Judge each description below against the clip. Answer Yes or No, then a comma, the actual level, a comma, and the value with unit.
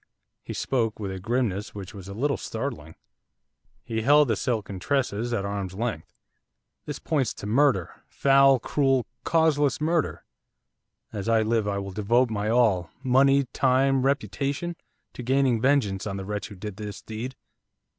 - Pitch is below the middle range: Yes, low, 115 Hz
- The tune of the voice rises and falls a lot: No, average, 5.0 semitones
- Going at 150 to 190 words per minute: Yes, average, 155 wpm